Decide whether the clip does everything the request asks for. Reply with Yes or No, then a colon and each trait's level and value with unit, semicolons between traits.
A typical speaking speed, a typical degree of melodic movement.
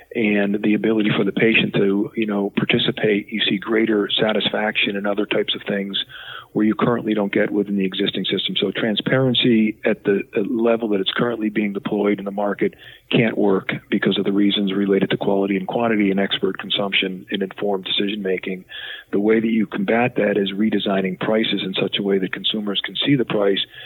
No: average, 195 wpm; narrow, 1.6 semitones